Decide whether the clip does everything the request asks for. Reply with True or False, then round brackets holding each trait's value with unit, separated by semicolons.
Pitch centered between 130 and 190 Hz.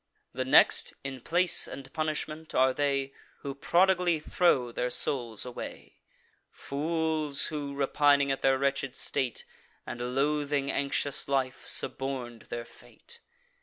True (140 Hz)